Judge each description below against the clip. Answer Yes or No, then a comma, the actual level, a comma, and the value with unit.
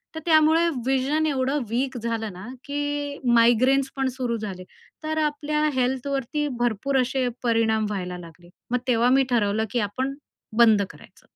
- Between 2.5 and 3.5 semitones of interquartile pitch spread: No, average, 4.1 semitones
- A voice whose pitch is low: No, very high, 255 Hz